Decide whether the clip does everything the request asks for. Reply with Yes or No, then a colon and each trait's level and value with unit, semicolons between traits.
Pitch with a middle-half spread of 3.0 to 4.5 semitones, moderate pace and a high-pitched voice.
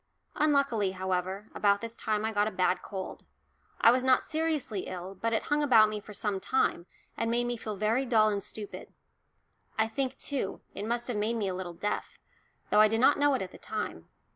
No: average, 3.4 semitones; fast, 215 wpm; high, 215 Hz